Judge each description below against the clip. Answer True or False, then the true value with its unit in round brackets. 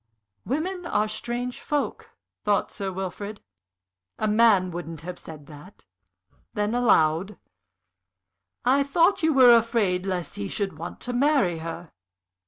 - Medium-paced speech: False (130 wpm)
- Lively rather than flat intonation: True (5.7 semitones)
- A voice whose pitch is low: False (210 Hz)